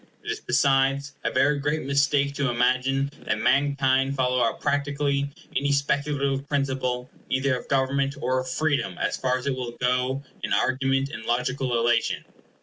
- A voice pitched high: No, low, 135 Hz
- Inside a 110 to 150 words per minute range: No, average, 160 wpm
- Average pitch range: No, narrow, 1.6 semitones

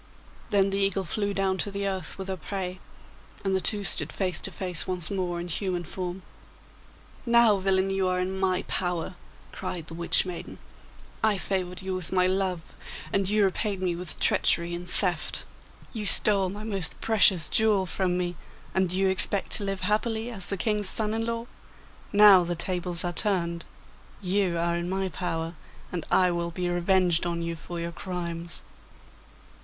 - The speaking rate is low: No, average, 180 wpm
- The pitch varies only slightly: Yes, narrow, 2.0 semitones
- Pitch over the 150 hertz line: Yes, medium, 185 Hz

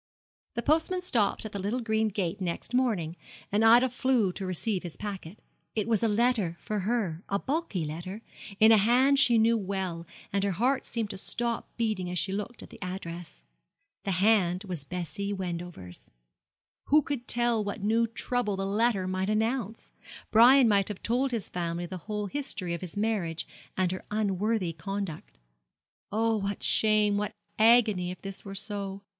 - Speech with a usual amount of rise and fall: Yes, average, 3.7 semitones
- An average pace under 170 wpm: No, average, 175 wpm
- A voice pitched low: No, high, 205 Hz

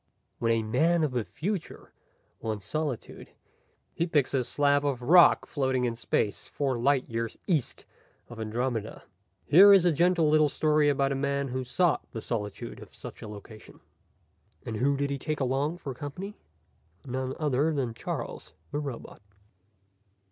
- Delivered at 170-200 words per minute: No, average, 160 wpm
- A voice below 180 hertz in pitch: Yes, medium, 140 Hz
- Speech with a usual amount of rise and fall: Yes, average, 4.2 semitones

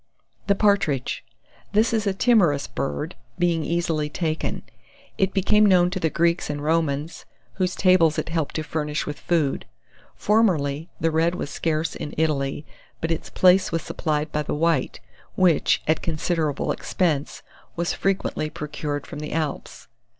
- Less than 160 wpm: Yes, average, 150 wpm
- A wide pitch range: No, average, 3.2 semitones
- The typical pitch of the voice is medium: Yes, medium, 165 Hz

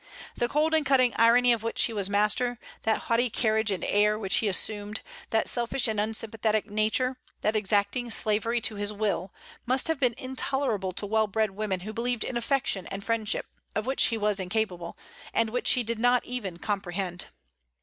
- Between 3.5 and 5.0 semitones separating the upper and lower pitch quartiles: No, average, 2.8 semitones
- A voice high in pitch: Yes, high, 220 Hz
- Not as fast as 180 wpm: No, average, 185 wpm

